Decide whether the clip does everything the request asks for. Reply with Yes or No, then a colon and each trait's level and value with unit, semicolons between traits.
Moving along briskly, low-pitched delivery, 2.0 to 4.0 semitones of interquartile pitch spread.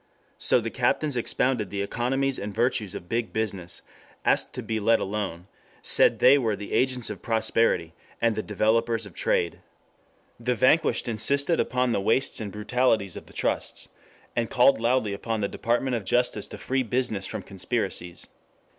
No: average, 165 wpm; low, 115 Hz; average, 3.4 semitones